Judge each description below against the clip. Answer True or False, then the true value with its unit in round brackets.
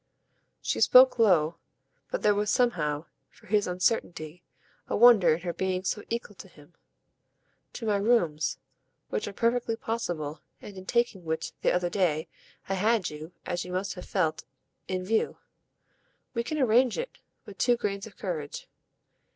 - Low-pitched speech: False (195 Hz)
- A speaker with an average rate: True (160 wpm)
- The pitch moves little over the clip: False (4.9 semitones)